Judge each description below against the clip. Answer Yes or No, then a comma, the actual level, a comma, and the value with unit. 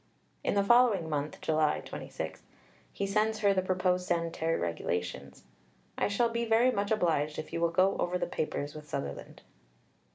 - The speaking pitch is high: No, medium, 180 Hz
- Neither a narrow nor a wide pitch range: Yes, average, 4.7 semitones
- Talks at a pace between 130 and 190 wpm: Yes, average, 165 wpm